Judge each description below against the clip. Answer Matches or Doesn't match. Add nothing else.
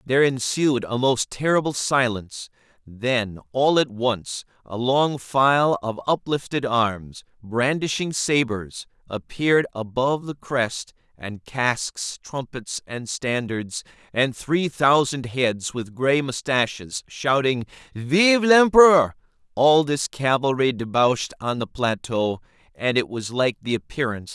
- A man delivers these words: Matches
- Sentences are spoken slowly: Matches